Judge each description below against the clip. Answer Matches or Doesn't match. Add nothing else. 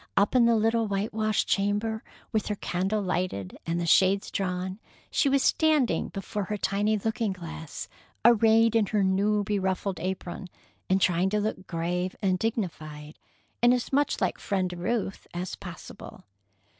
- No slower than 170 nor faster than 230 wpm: Doesn't match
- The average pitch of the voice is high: Matches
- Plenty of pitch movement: Doesn't match